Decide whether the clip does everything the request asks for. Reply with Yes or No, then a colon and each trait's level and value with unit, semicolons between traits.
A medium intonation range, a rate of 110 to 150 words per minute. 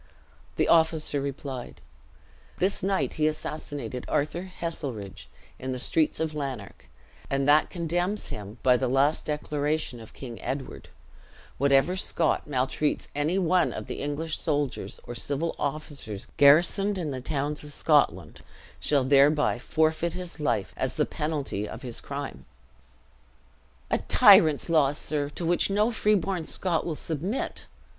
Yes: average, 3.2 semitones; average, 140 wpm